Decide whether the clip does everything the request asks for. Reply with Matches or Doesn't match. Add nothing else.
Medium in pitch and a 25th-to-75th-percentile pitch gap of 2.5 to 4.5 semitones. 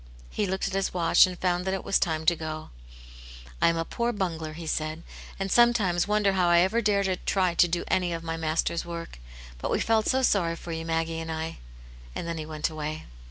Matches